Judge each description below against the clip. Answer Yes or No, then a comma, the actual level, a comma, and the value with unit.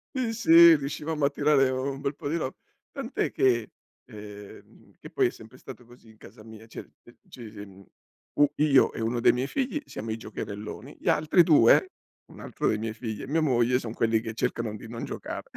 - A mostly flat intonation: No, average, 4.9 semitones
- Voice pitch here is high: No, low, 125 Hz